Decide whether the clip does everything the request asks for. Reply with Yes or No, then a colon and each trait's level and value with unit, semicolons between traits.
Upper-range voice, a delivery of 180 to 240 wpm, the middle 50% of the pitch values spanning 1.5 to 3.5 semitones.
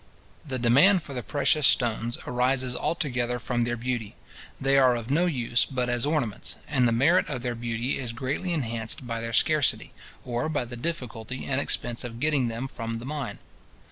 No: low, 125 Hz; average, 185 wpm; average, 2.9 semitones